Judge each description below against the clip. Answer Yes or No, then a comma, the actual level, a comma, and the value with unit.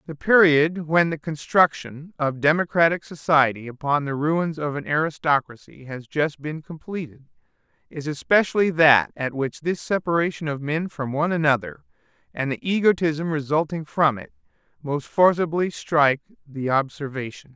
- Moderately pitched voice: Yes, medium, 155 Hz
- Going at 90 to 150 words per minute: Yes, average, 140 wpm